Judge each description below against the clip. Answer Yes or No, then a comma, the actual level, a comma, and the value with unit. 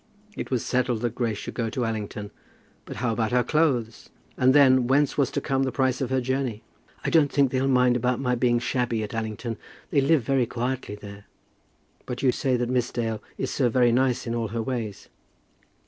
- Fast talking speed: Yes, fast, 210 wpm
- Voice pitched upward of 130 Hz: No, low, 125 Hz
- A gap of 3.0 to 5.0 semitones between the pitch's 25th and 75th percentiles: No, narrow, 2.4 semitones